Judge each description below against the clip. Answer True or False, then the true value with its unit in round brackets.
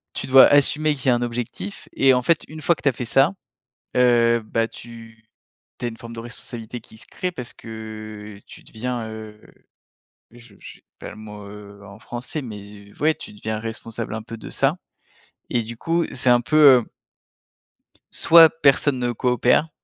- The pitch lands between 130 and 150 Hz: False (120 Hz)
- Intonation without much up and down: False (3.2 semitones)